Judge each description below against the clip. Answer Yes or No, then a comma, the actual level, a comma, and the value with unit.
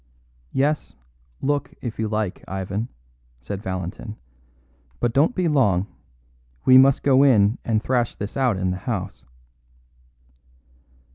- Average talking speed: No, slow, 125 wpm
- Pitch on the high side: No, low, 115 Hz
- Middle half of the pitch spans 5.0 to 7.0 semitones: Yes, average, 5.3 semitones